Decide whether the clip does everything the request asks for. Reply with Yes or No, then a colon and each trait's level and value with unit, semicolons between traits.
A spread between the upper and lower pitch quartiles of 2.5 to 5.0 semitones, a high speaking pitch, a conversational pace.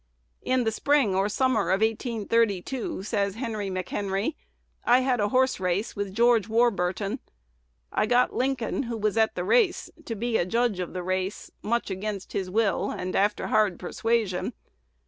Yes: average, 3.6 semitones; high, 215 Hz; average, 165 wpm